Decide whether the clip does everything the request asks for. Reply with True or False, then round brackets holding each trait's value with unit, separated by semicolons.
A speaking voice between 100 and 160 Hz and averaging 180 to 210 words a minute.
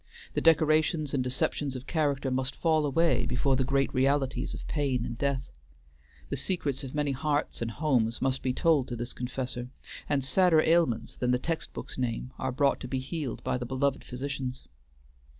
True (135 Hz; 185 wpm)